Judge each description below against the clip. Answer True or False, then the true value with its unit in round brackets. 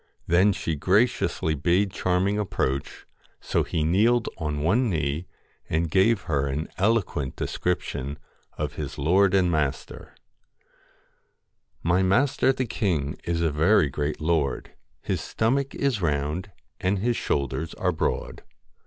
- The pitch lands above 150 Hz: False (85 Hz)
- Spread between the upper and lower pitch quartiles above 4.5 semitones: True (5.2 semitones)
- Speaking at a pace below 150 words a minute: True (135 wpm)